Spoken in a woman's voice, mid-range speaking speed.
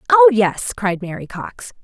Yes: female; average, 165 wpm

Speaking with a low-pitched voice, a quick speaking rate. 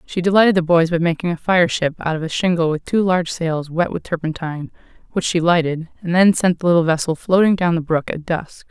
No: medium, 170 Hz; fast, 240 wpm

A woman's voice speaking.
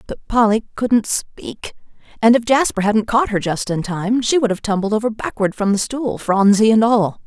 Yes: female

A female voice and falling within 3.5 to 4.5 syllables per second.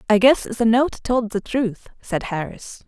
Yes: female; 4.0 syllables/s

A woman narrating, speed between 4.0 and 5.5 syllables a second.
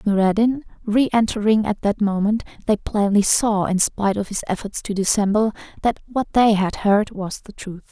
Yes: female; 5.0 syllables/s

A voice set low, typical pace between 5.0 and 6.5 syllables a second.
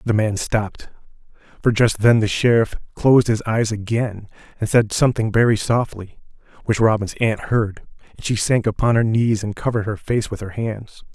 Yes: low, 110 Hz; 5.1 syllables/s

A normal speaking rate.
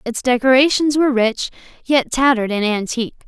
Yes: average, 145 wpm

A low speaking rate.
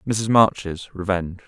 Yes: slow, 120 wpm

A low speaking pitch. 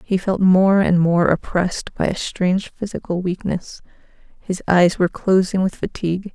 No: medium, 185 Hz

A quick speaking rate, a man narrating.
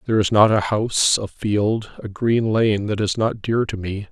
Yes: fast, 235 wpm; male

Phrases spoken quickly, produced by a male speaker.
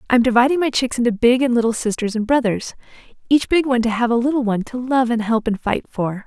No: fast, 250 wpm; female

